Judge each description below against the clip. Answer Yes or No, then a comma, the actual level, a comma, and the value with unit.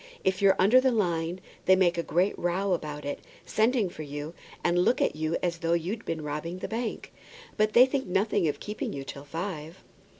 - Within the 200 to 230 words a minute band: Yes, fast, 205 wpm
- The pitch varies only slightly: No, average, 4.0 semitones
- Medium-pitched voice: Yes, medium, 175 Hz